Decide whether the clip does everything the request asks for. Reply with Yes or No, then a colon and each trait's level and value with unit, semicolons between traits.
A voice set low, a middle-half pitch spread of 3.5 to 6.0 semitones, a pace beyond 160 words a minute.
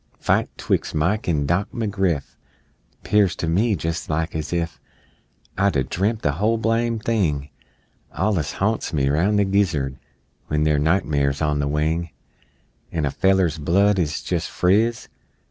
No: very low, 85 Hz; average, 5.2 semitones; average, 150 wpm